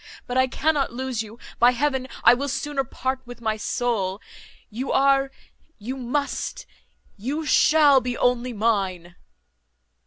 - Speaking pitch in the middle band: No, very high, 250 Hz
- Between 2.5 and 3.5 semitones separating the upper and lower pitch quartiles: Yes, average, 2.8 semitones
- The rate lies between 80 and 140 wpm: Yes, slow, 135 wpm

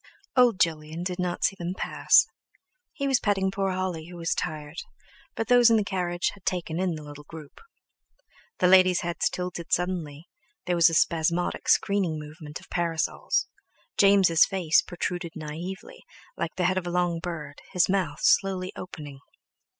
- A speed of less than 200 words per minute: Yes, average, 165 wpm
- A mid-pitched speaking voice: Yes, medium, 175 Hz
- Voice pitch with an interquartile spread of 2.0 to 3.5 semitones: Yes, narrow, 2.6 semitones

